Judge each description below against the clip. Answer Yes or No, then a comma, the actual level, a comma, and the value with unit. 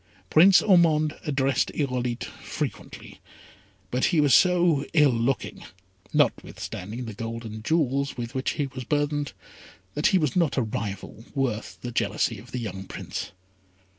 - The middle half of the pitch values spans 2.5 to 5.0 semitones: Yes, average, 4.5 semitones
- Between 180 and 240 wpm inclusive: No, average, 145 wpm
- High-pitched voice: No, low, 135 Hz